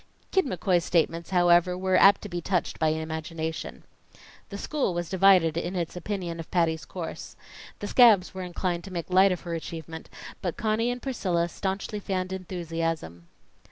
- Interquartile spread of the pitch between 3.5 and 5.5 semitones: No, narrow, 2.5 semitones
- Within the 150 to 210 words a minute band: Yes, average, 165 wpm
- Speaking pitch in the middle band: Yes, medium, 180 Hz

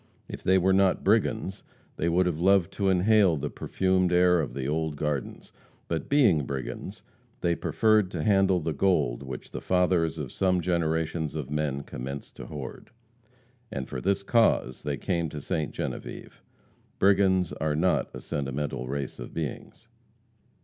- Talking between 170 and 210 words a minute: No, average, 160 wpm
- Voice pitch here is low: Yes, very low, 85 Hz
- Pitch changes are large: No, average, 4.4 semitones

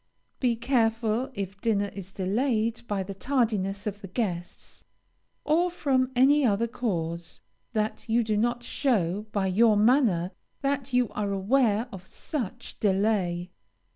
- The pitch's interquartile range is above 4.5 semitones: No, average, 4.1 semitones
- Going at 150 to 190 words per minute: No, average, 140 wpm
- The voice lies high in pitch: Yes, high, 215 Hz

